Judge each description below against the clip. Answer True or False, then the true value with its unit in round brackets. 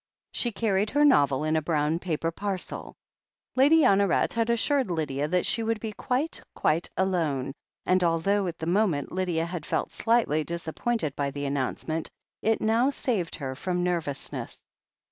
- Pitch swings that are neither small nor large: False (6.0 semitones)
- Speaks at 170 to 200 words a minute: False (160 wpm)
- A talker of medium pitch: True (175 Hz)